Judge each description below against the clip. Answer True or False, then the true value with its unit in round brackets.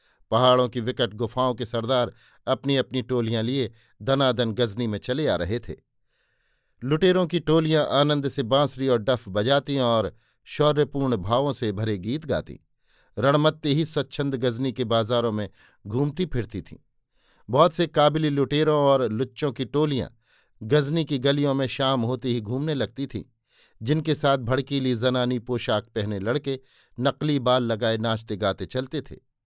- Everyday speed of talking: True (155 wpm)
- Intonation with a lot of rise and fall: False (3.3 semitones)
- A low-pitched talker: True (130 Hz)